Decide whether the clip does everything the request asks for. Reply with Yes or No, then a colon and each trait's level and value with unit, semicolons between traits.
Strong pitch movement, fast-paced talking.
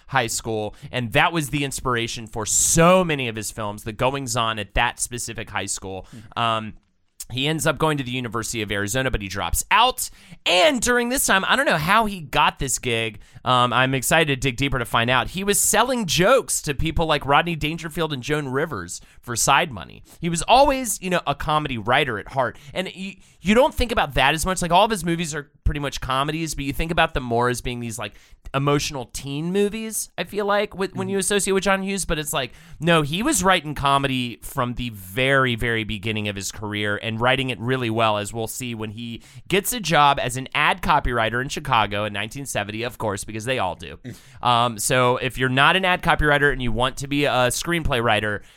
Yes: wide, 6.1 semitones; fast, 225 wpm